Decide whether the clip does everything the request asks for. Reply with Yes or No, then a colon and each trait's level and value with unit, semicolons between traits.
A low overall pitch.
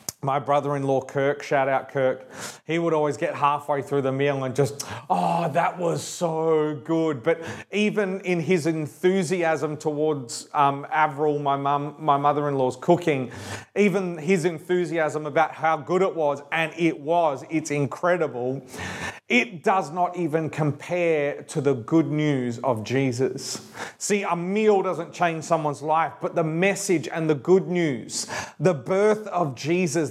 No: medium, 155 Hz